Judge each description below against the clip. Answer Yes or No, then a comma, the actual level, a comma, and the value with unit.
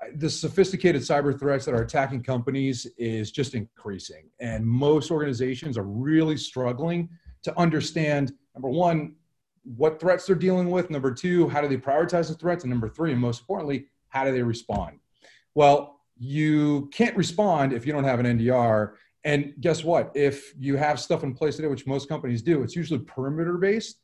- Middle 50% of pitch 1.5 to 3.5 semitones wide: No, average, 4.0 semitones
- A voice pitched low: No, medium, 145 Hz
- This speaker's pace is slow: No, average, 180 wpm